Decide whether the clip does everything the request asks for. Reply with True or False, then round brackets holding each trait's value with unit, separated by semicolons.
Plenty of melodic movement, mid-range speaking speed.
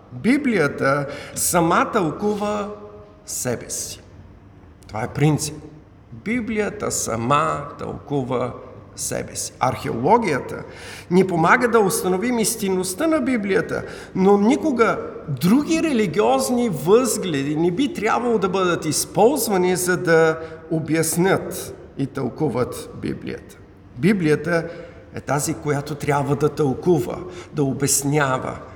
False (7.1 semitones; 100 wpm)